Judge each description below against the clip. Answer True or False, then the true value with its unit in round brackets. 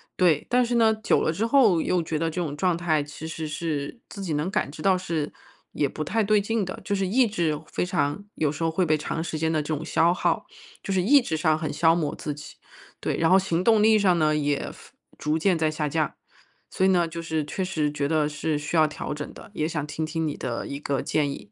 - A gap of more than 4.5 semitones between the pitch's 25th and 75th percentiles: False (3.6 semitones)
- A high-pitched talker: False (160 Hz)